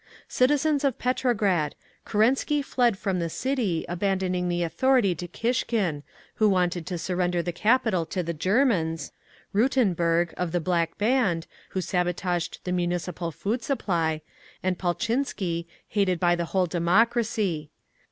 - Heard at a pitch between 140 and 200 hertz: Yes, medium, 185 Hz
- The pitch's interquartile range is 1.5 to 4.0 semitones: No, average, 5.0 semitones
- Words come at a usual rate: No, slow, 130 wpm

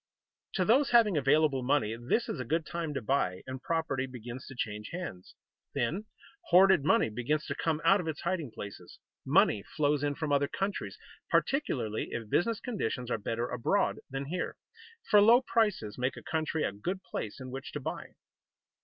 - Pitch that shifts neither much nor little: No, wide, 6.3 semitones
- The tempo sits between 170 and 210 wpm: Yes, average, 180 wpm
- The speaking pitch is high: No, medium, 145 Hz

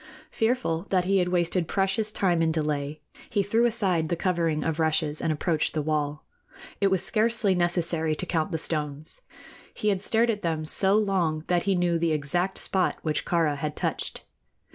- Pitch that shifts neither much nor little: Yes, average, 3.7 semitones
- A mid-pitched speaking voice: Yes, medium, 170 Hz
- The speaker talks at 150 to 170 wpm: No, average, 185 wpm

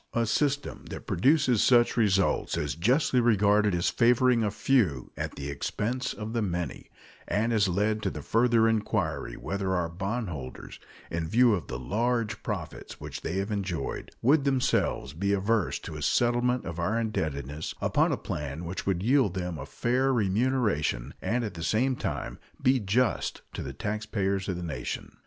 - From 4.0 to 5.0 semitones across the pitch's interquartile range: No, wide, 5.4 semitones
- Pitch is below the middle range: Yes, low, 105 Hz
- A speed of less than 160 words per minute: No, average, 170 wpm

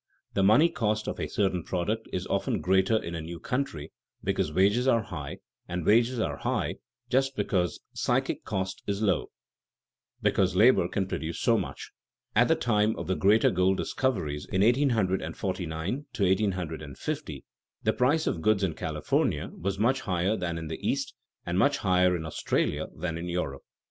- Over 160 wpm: Yes, average, 170 wpm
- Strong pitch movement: No, average, 4.2 semitones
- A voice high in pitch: No, very low, 95 Hz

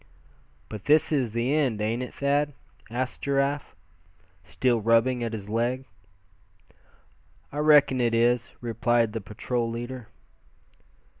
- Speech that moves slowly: Yes, slow, 125 wpm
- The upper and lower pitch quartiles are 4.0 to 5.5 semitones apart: No, average, 3.0 semitones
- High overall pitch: No, low, 120 Hz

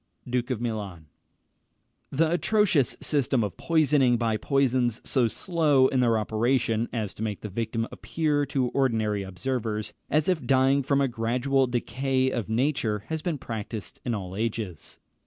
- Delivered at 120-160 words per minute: Yes, average, 155 wpm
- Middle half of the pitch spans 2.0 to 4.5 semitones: Yes, average, 3.9 semitones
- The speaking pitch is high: No, low, 125 Hz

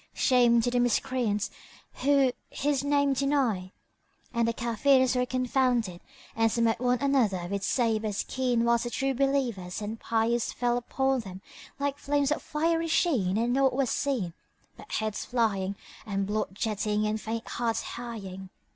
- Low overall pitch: No, high, 235 Hz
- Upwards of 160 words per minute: No, average, 155 wpm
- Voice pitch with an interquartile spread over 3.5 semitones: Yes, average, 3.9 semitones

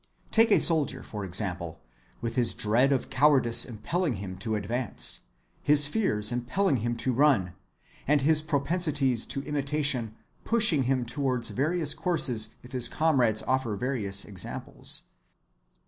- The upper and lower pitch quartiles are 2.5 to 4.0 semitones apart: No, average, 5.0 semitones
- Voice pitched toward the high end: No, low, 130 Hz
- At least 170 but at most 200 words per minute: No, slow, 135 wpm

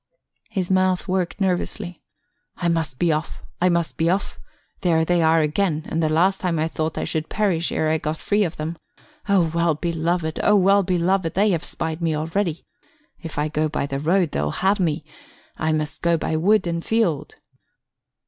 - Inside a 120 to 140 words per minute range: No, average, 190 wpm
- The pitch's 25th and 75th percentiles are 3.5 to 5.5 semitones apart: No, average, 2.8 semitones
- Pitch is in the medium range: Yes, medium, 170 Hz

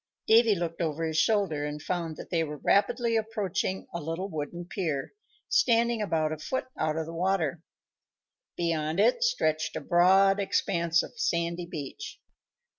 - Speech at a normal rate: Yes, average, 155 wpm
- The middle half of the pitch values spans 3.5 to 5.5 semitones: Yes, average, 4.1 semitones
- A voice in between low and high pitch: Yes, medium, 170 Hz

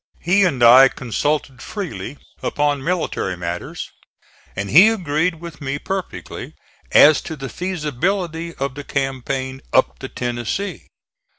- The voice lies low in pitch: No, medium, 145 Hz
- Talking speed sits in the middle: No, slow, 125 wpm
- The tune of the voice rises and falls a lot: No, average, 4.7 semitones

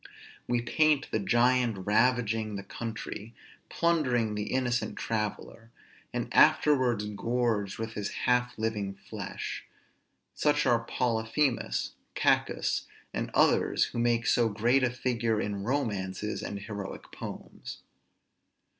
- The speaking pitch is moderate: No, low, 115 Hz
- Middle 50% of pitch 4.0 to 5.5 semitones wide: No, average, 2.7 semitones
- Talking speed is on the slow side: Yes, slow, 115 wpm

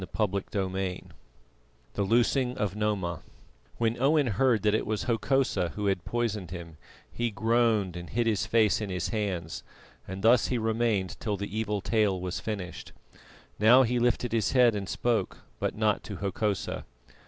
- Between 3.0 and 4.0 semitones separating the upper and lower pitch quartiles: Yes, average, 3.4 semitones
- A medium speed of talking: Yes, average, 165 wpm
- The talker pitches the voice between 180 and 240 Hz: No, low, 105 Hz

